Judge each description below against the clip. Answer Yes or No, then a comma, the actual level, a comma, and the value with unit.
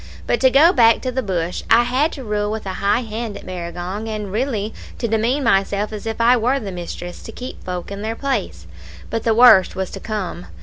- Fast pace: Yes, fast, 225 wpm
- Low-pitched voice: No, high, 220 Hz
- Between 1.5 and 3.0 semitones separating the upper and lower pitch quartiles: No, average, 3.8 semitones